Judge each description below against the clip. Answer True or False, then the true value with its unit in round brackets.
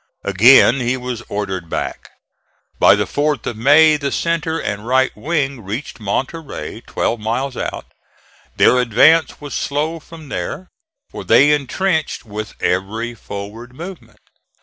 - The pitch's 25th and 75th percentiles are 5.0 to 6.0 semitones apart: True (5.5 semitones)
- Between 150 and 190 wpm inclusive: False (135 wpm)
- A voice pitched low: True (130 Hz)